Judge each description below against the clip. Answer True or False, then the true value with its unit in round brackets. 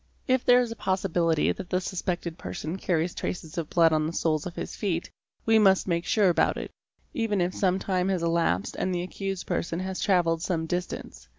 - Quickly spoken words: True (210 wpm)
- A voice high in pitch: False (180 Hz)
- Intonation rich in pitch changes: False (2.5 semitones)